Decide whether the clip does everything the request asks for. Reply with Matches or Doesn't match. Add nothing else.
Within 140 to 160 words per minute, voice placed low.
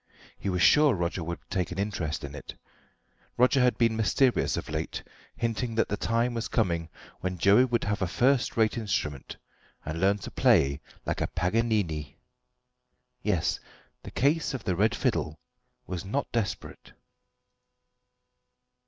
Matches